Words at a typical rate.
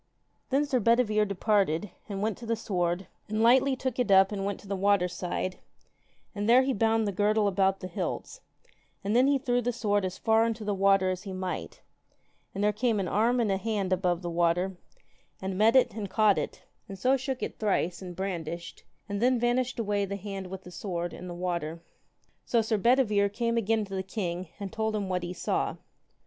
No: fast, 210 wpm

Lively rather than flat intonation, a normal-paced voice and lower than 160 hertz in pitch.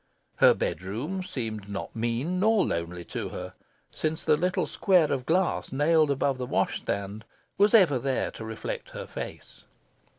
Yes: wide, 7.9 semitones; average, 160 wpm; low, 135 Hz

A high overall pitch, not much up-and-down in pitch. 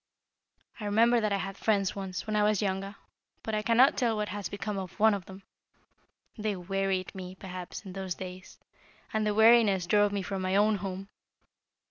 Yes: high, 200 Hz; narrow, 2.0 semitones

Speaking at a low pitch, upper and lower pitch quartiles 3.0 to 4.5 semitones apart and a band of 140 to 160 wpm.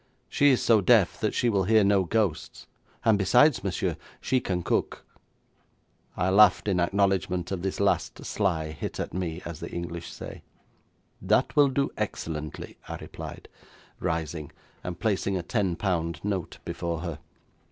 Yes: very low, 95 Hz; average, 3.5 semitones; average, 155 wpm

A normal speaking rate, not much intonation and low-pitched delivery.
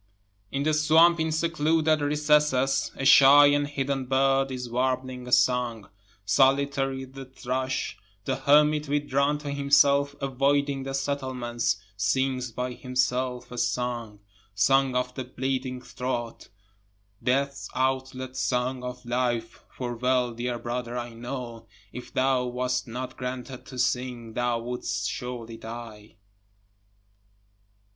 No: slow, 125 wpm; narrow, 2.0 semitones; low, 130 Hz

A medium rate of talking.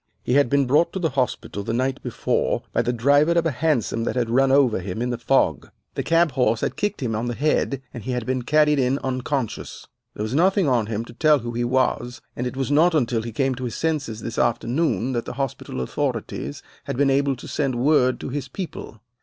No: fast, 235 wpm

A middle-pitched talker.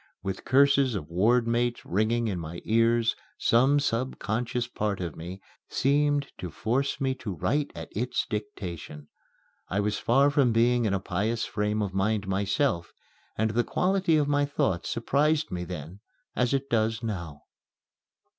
No: low, 115 Hz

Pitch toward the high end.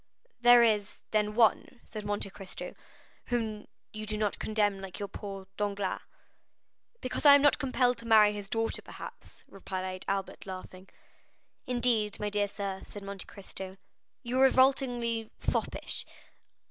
Yes: high, 210 Hz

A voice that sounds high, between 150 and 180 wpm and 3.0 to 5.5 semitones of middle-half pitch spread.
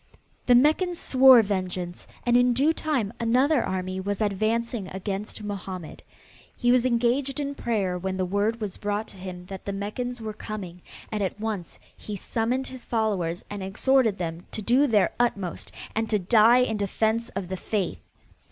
Yes: high, 215 Hz; average, 170 wpm; average, 4.2 semitones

